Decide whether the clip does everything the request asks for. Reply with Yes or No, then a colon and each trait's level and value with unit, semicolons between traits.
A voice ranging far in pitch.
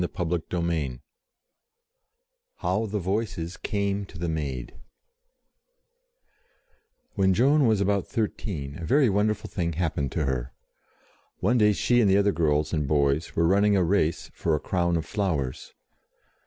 No: average, 4.6 semitones